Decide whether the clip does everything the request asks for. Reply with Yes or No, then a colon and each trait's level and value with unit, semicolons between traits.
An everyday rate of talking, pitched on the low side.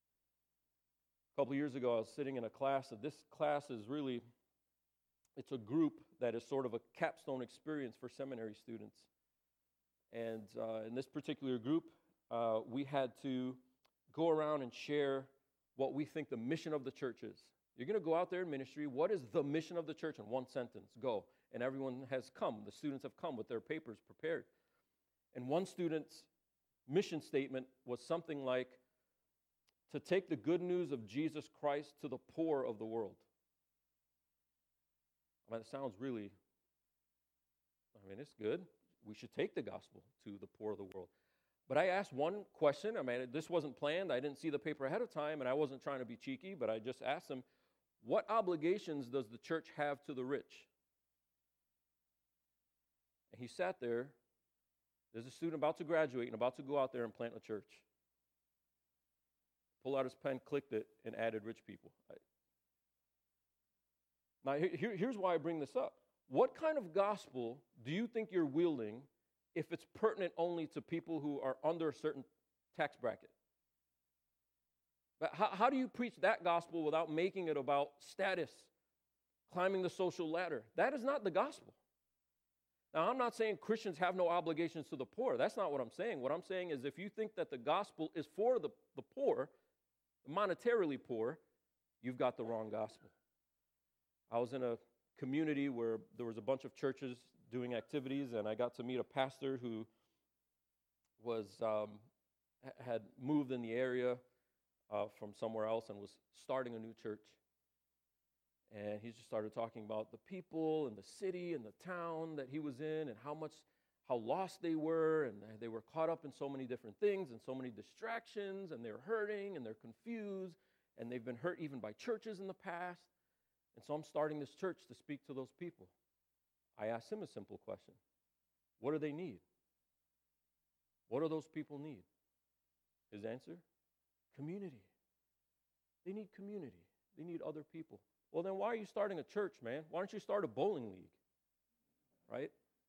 Yes: average, 180 wpm; low, 130 Hz